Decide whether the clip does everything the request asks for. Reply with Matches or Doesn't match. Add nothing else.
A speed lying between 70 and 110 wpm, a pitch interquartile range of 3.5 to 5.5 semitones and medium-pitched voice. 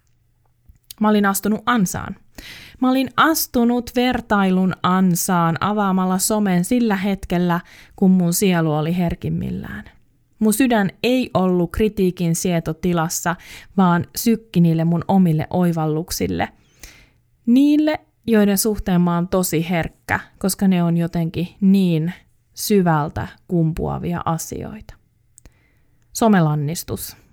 Matches